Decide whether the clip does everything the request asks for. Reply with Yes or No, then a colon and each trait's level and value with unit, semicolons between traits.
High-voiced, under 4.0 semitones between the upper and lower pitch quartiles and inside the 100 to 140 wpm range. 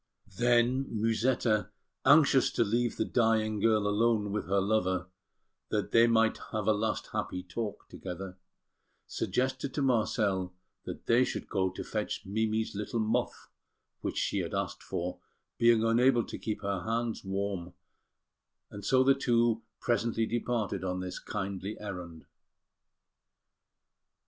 No: low, 110 Hz; average, 3.1 semitones; slow, 135 wpm